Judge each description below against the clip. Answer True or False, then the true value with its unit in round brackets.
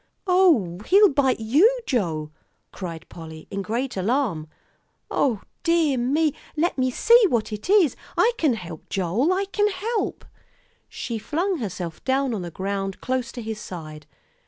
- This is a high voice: True (245 Hz)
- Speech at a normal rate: True (155 wpm)